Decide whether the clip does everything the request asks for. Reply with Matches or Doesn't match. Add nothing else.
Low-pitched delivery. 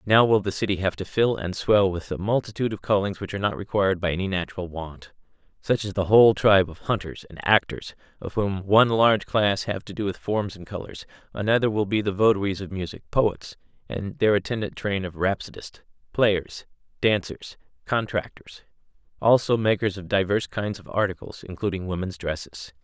Matches